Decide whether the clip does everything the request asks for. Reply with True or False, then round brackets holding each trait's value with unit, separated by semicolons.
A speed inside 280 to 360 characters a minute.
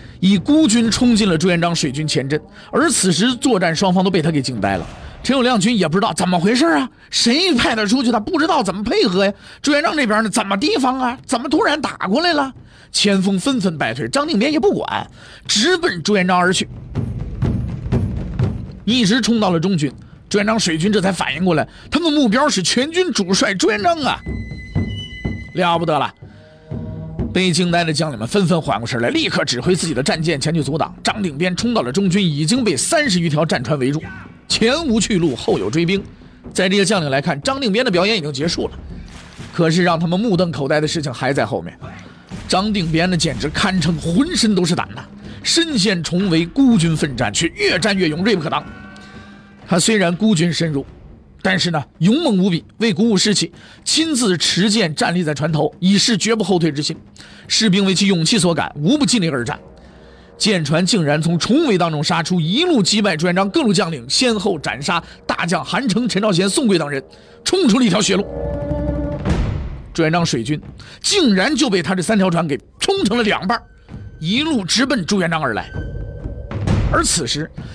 True (285 characters per minute)